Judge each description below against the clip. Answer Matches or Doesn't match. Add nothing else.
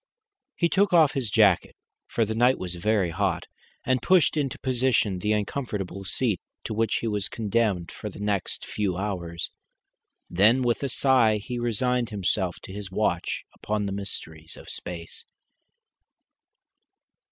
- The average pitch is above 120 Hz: Doesn't match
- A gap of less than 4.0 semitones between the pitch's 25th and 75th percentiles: Doesn't match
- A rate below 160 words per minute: Matches